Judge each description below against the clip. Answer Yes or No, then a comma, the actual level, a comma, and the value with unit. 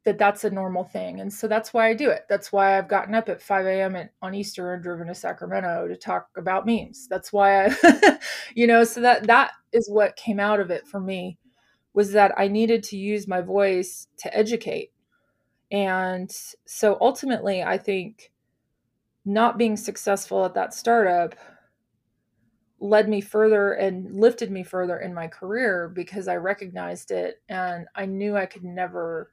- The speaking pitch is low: No, high, 200 Hz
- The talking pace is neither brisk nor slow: Yes, average, 180 wpm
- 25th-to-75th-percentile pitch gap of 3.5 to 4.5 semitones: No, average, 2.9 semitones